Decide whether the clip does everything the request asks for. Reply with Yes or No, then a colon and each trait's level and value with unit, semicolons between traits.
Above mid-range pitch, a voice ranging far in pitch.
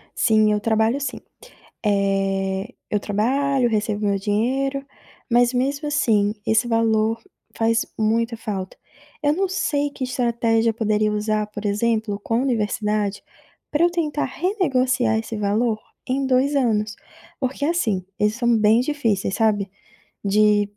No: high, 225 Hz; average, 3.5 semitones